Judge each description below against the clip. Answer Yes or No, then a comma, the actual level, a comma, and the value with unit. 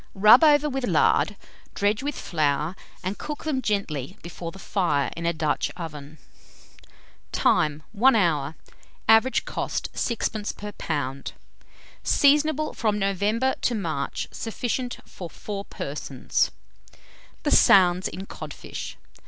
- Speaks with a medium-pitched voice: No, high, 195 Hz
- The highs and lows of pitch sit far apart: Yes, wide, 6.8 semitones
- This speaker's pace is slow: Yes, slow, 120 wpm